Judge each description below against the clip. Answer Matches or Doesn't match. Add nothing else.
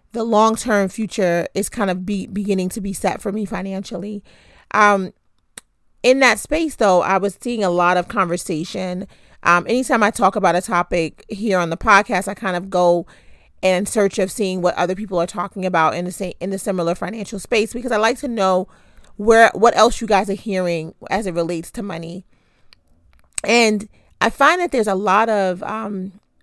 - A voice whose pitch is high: Matches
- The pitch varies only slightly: Doesn't match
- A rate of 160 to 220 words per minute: Matches